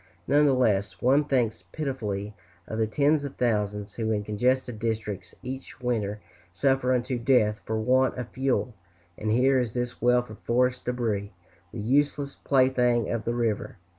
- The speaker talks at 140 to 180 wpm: Yes, average, 155 wpm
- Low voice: Yes, low, 120 Hz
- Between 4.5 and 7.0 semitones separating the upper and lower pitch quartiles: No, average, 3.3 semitones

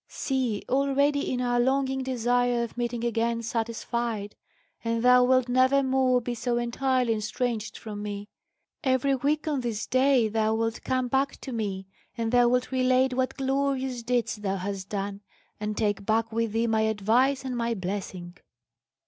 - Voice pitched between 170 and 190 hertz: No, high, 240 Hz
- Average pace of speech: Yes, average, 165 wpm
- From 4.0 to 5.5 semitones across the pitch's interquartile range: No, average, 2.8 semitones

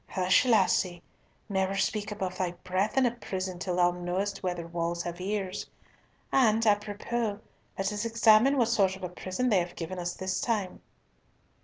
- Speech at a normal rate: Yes, average, 170 wpm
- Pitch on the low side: No, high, 190 Hz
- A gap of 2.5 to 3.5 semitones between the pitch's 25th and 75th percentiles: Yes, average, 2.9 semitones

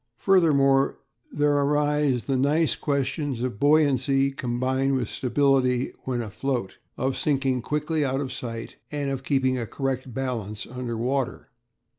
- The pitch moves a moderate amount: No, narrow, 2.1 semitones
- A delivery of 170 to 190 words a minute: No, slow, 135 wpm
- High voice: No, low, 135 Hz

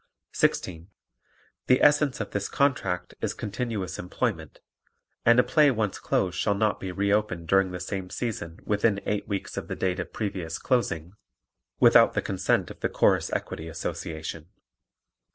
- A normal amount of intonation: Yes, average, 3.6 semitones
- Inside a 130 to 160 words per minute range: Yes, average, 155 wpm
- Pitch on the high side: No, low, 100 Hz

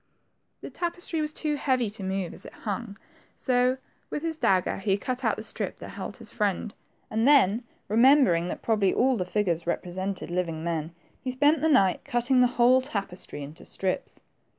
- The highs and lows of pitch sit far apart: Yes, wide, 5.8 semitones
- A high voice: Yes, high, 220 Hz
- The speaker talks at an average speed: Yes, average, 180 wpm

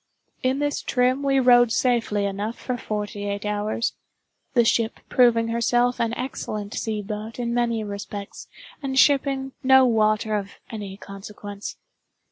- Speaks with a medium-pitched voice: No, high, 230 Hz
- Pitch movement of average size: Yes, average, 3.2 semitones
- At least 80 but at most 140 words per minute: Yes, slow, 135 wpm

